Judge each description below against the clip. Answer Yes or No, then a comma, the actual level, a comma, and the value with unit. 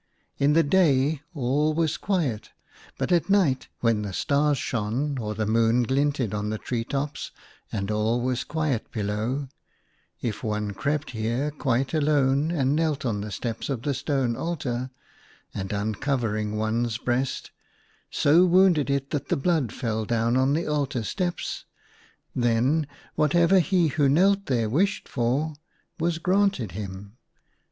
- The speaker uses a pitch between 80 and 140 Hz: Yes, low, 135 Hz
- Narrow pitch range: No, average, 5.0 semitones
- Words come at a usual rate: Yes, average, 145 wpm